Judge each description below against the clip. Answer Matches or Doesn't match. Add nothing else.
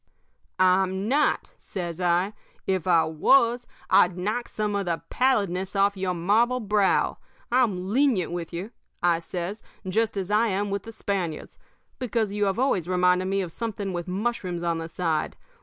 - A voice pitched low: Doesn't match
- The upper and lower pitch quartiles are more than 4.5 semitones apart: Doesn't match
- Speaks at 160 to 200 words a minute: Matches